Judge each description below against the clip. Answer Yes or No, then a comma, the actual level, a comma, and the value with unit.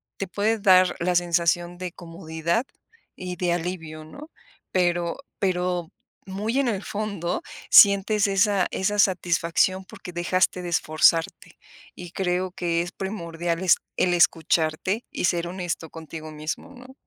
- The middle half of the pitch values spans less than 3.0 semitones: Yes, narrow, 2.4 semitones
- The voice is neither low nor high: Yes, medium, 180 Hz